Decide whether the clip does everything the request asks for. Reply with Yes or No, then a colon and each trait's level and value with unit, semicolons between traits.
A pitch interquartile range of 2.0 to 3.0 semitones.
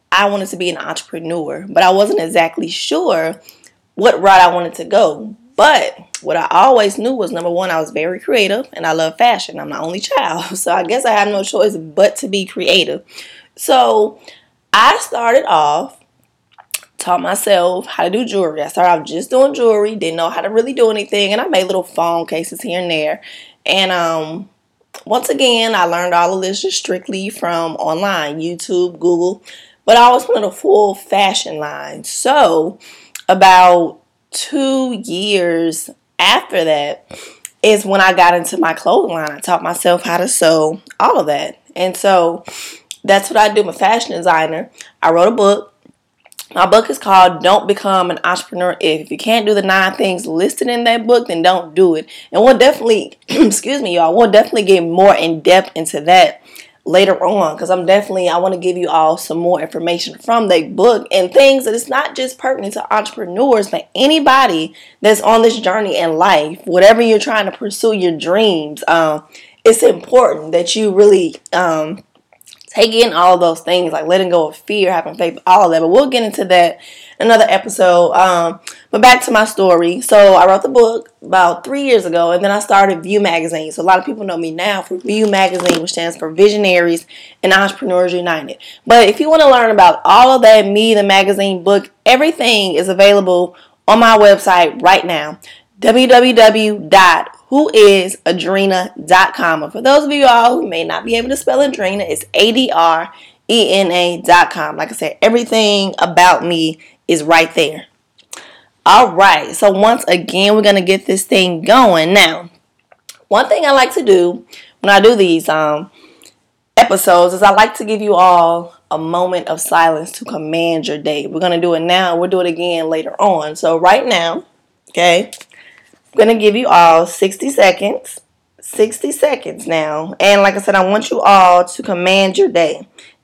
No: average, 4.2 semitones